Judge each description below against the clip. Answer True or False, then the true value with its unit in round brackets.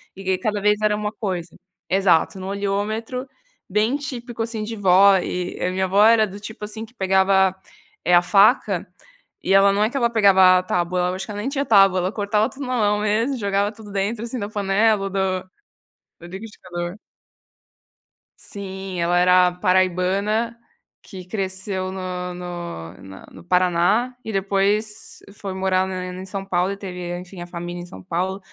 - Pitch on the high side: True (195 Hz)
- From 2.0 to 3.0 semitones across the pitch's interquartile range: True (2.5 semitones)